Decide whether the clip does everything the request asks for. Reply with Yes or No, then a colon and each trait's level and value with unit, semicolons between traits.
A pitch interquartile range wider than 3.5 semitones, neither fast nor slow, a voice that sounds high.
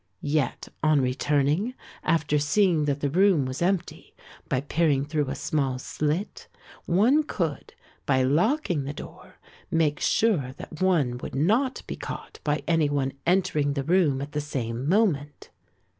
No: average, 4.1 semitones; average, 150 wpm; medium, 150 Hz